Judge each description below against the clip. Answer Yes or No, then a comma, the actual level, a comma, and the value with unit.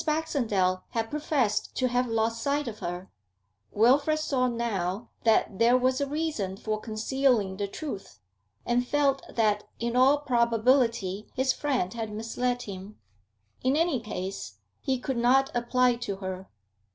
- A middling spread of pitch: Yes, average, 4.0 semitones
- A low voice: No, high, 235 Hz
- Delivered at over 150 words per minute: No, average, 145 wpm